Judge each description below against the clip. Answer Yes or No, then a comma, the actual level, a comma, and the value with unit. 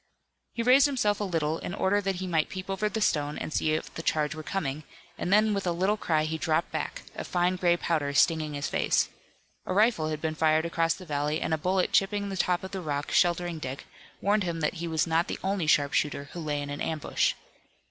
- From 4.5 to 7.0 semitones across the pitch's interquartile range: No, average, 3.7 semitones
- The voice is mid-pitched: Yes, medium, 170 Hz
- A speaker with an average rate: No, fast, 235 wpm